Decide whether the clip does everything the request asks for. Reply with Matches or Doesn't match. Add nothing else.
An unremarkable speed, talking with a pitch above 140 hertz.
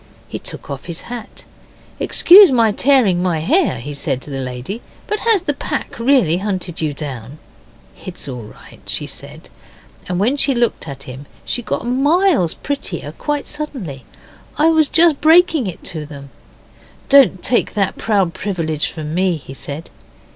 Matches